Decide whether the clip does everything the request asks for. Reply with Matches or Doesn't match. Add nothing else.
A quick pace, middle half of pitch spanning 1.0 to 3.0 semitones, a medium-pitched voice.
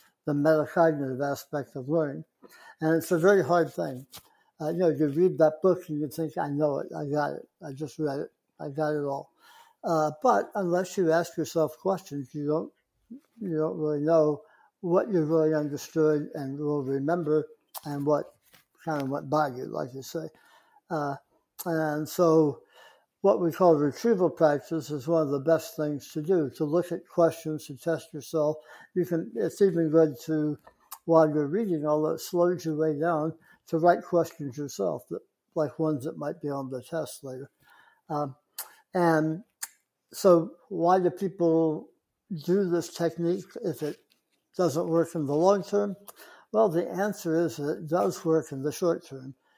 Doesn't match